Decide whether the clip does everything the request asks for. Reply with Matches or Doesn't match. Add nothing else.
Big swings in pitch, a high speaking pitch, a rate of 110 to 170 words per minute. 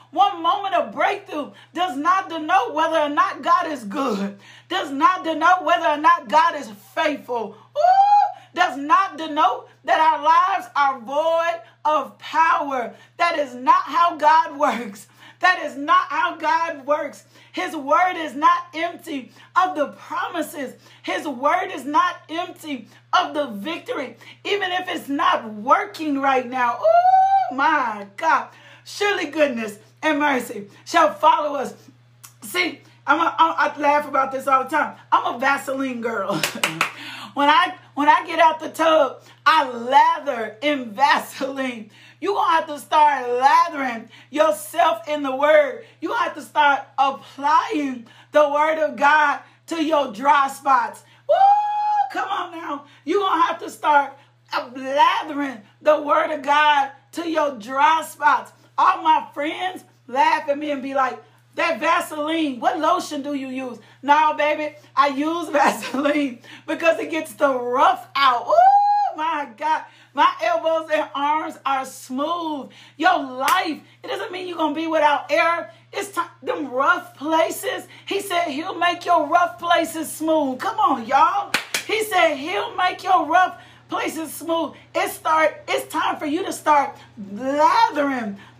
Doesn't match